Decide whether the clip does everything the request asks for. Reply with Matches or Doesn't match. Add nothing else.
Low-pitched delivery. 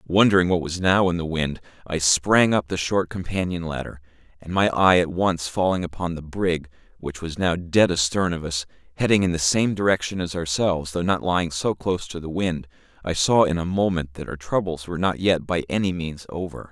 Matches